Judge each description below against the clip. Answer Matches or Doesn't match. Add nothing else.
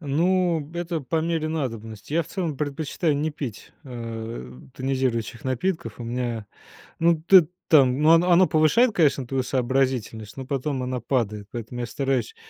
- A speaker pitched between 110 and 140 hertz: Matches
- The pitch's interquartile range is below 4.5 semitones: Doesn't match